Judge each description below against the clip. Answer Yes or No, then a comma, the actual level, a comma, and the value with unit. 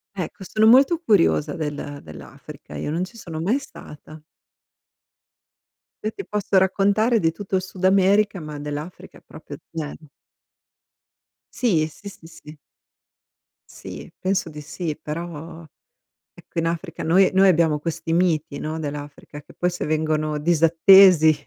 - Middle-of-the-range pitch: Yes, medium, 165 Hz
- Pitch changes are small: No, average, 3.9 semitones